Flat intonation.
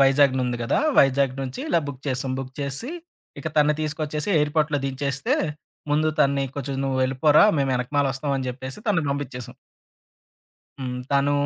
Yes: narrow, 2.0 semitones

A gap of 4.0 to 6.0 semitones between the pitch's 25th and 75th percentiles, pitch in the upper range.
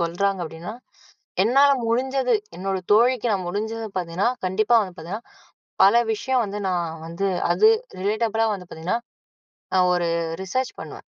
Yes: average, 4.5 semitones; high, 200 Hz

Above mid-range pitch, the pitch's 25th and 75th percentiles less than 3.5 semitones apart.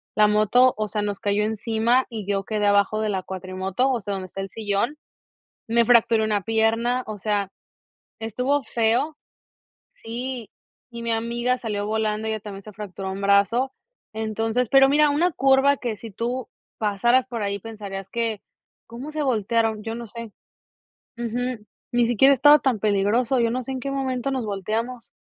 Yes: high, 225 Hz; average, 3.1 semitones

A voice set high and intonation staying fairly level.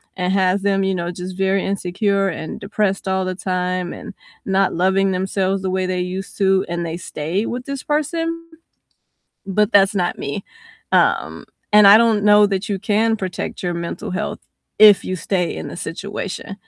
Yes: high, 195 Hz; narrow, 2.0 semitones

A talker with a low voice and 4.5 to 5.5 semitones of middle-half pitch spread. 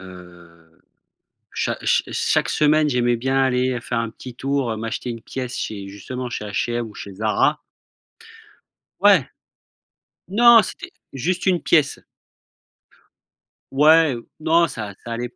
Yes: low, 125 Hz; average, 5.2 semitones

